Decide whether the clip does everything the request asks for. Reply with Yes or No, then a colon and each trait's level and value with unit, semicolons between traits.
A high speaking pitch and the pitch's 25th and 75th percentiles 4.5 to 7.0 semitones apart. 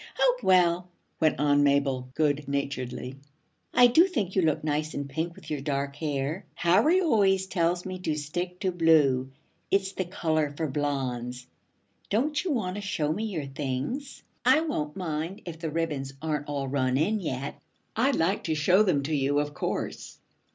No: medium, 155 Hz; average, 4.8 semitones